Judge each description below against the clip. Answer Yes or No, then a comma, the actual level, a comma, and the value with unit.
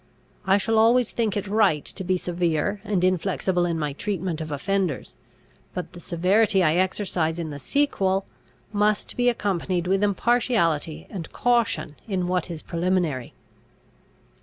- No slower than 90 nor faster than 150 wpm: Yes, average, 145 wpm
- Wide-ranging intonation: No, average, 3.6 semitones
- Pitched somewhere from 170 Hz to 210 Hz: Yes, medium, 185 Hz